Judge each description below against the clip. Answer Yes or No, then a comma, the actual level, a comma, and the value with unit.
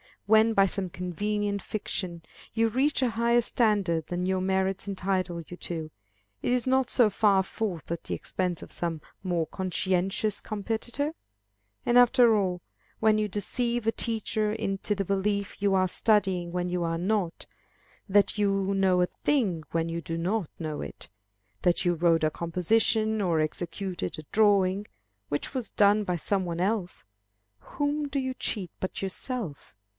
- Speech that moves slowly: No, average, 165 wpm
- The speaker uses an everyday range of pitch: Yes, average, 3.7 semitones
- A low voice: No, high, 195 Hz